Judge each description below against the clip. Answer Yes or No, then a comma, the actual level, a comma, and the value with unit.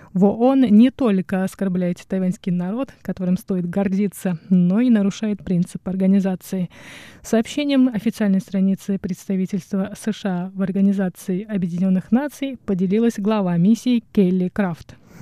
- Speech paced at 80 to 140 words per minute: Yes, slow, 110 wpm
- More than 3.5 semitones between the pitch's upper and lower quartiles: No, narrow, 2.5 semitones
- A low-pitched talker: No, high, 195 Hz